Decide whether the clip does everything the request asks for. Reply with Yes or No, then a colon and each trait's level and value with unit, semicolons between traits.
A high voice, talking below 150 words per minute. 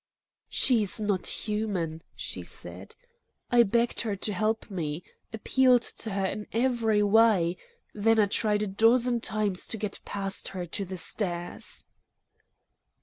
Yes: high, 210 Hz; average, 140 wpm